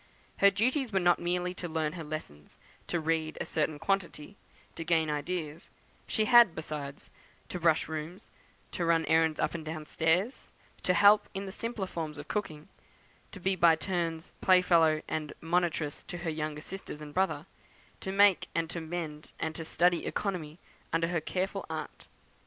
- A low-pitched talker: No, medium, 165 Hz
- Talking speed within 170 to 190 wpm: Yes, average, 175 wpm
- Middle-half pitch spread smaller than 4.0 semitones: Yes, average, 2.8 semitones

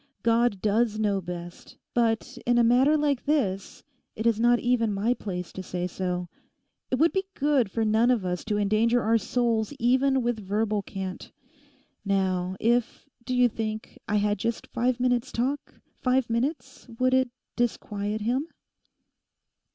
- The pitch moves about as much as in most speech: Yes, average, 3.3 semitones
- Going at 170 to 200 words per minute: No, average, 155 wpm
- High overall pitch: Yes, high, 230 Hz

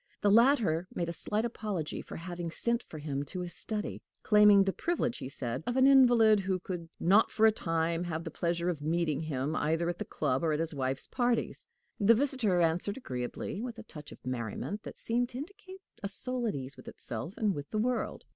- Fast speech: Yes, fast, 215 wpm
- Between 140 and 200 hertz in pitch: Yes, medium, 185 Hz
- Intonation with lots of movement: Yes, wide, 6.2 semitones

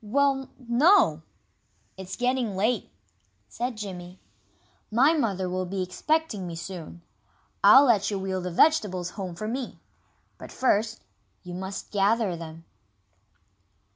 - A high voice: Yes, high, 200 Hz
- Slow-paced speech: Yes, slow, 125 wpm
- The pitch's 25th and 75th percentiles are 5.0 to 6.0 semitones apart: Yes, average, 5.3 semitones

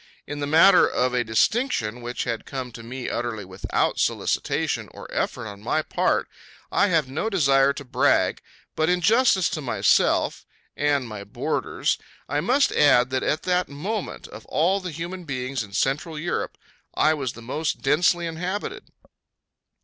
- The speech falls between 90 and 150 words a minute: No, average, 165 wpm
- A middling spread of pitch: No, wide, 6.1 semitones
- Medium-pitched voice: Yes, medium, 145 Hz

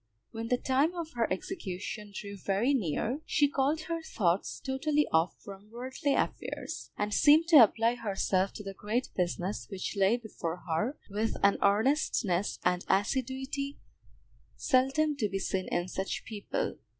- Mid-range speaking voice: No, high, 225 Hz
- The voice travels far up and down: Yes, wide, 5.8 semitones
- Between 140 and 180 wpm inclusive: Yes, average, 150 wpm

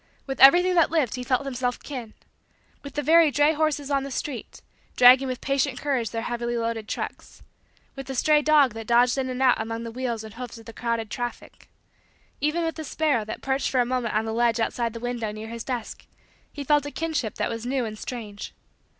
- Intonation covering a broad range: No, average, 3.5 semitones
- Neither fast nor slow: No, fast, 220 wpm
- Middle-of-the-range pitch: No, very high, 250 Hz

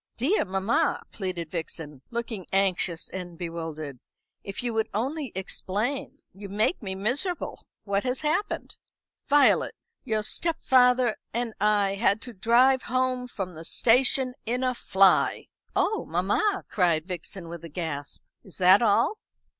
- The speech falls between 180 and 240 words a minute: No, average, 140 wpm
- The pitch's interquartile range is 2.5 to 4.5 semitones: No, wide, 5.6 semitones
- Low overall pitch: No, high, 210 Hz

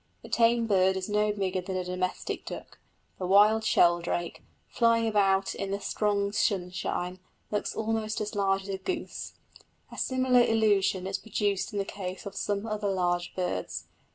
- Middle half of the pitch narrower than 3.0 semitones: Yes, narrow, 2.4 semitones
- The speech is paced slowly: No, average, 165 wpm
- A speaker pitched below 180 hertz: No, high, 200 Hz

